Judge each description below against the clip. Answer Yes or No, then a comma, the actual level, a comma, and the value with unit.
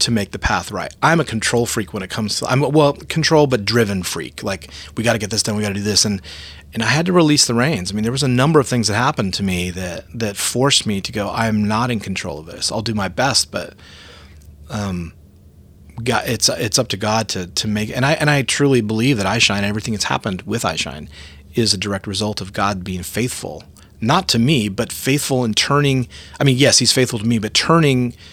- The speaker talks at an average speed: No, fast, 250 wpm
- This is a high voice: No, low, 110 Hz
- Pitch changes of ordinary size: Yes, average, 4.7 semitones